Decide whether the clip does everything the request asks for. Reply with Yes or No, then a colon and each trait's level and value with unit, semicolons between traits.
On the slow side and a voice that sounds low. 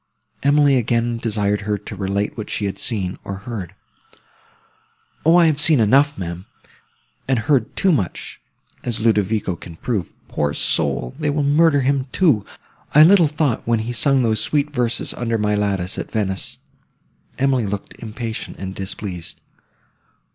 No: average, 150 wpm; low, 115 Hz